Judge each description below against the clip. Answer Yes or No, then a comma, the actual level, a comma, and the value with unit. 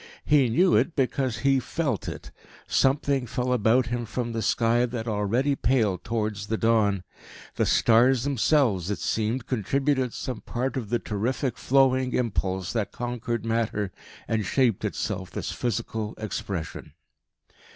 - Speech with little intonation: No, average, 3.2 semitones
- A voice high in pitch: No, low, 120 Hz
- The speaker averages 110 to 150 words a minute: Yes, average, 140 wpm